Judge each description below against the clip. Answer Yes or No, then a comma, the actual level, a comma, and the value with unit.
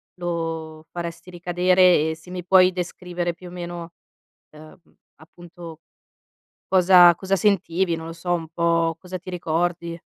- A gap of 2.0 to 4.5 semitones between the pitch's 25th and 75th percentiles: No, narrow, 1.5 semitones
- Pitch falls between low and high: Yes, medium, 175 Hz